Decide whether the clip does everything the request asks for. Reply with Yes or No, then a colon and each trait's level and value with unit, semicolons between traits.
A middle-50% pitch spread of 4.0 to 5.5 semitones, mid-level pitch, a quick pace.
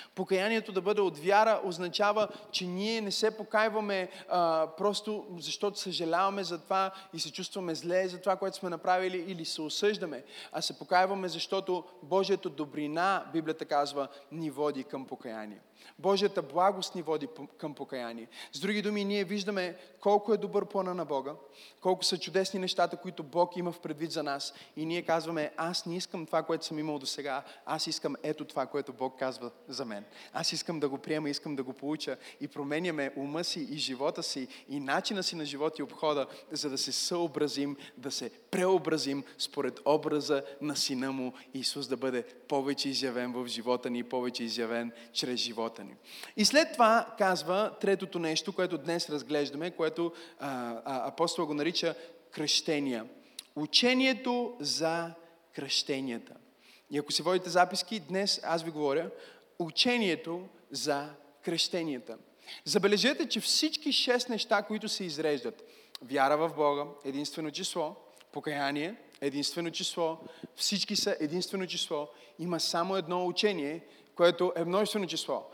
No: average, 4.6 semitones; medium, 165 Hz; average, 155 wpm